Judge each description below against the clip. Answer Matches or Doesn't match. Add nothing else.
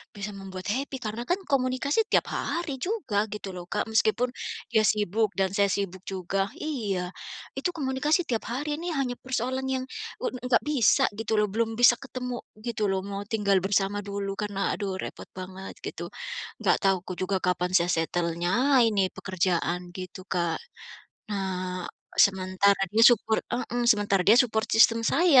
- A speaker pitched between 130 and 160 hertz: Doesn't match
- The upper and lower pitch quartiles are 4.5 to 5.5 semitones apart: Matches